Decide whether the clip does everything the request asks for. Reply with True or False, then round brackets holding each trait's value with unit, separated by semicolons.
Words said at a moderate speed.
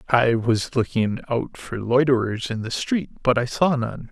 True (190 wpm)